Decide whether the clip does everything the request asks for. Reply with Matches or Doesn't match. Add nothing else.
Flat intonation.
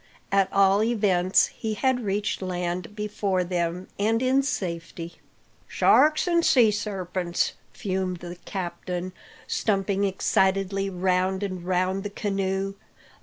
Matches